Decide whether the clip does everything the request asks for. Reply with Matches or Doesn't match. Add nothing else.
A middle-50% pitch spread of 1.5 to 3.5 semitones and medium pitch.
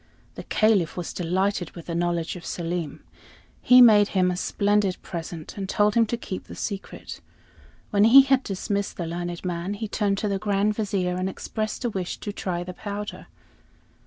Doesn't match